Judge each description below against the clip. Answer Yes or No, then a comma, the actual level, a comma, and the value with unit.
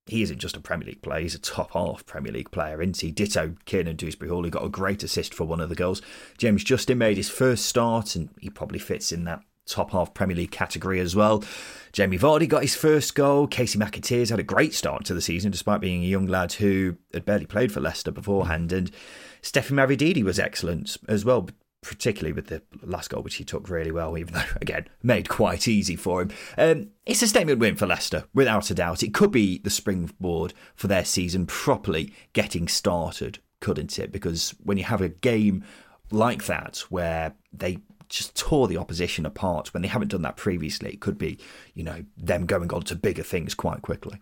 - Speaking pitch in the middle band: No, low, 100 Hz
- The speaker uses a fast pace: Yes, fast, 215 wpm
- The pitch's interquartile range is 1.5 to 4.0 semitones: No, average, 4.4 semitones